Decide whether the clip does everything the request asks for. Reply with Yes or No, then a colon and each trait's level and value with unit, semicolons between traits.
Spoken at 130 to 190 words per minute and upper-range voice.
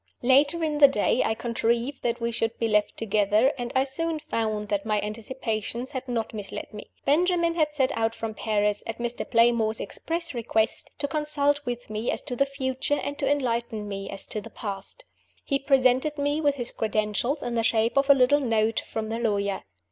No: average, 200 wpm; high, 240 Hz